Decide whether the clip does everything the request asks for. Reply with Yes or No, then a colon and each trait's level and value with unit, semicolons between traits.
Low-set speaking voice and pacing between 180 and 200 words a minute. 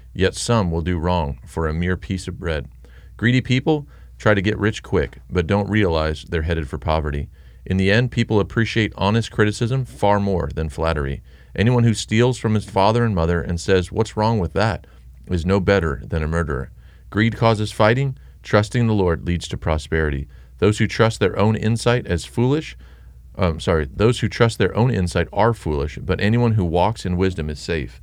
Yes: very low, 95 Hz; average, 190 wpm